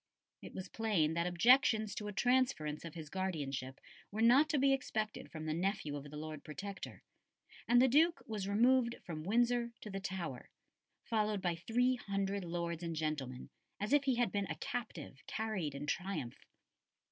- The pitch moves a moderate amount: No, wide, 6.7 semitones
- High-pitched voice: Yes, high, 195 Hz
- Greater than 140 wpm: Yes, average, 175 wpm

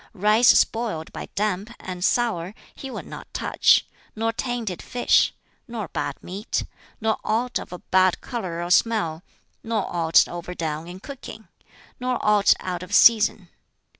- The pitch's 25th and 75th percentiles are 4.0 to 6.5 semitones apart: Yes, average, 4.5 semitones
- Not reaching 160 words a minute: Yes, average, 145 wpm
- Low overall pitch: No, high, 210 Hz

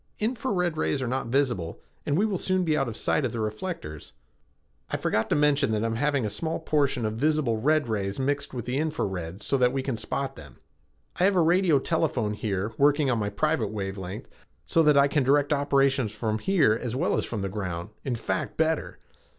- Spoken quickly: Yes, fast, 220 wpm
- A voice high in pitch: No, low, 135 Hz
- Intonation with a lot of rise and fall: Yes, wide, 6.0 semitones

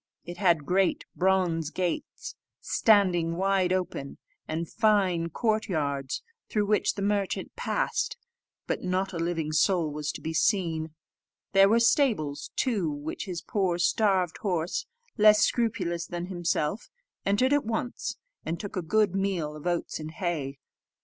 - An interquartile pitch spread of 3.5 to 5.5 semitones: Yes, average, 3.8 semitones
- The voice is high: No, medium, 180 Hz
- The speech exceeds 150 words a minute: No, average, 145 wpm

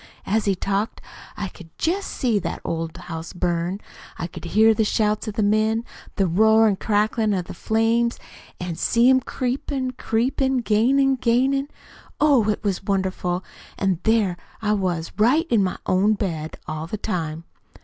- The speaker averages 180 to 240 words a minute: No, average, 165 wpm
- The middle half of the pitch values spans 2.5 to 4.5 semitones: Yes, average, 4.2 semitones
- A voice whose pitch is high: Yes, high, 210 Hz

